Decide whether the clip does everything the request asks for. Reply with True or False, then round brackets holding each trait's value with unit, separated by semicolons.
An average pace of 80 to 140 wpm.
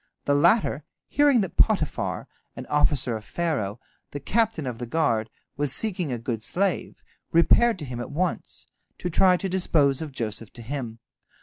False (170 wpm)